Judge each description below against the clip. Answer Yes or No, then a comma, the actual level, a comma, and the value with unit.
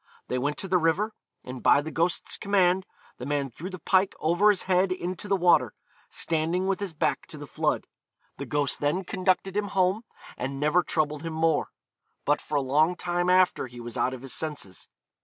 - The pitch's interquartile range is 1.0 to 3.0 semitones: No, average, 4.0 semitones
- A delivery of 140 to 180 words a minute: No, average, 200 wpm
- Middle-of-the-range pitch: Yes, medium, 170 Hz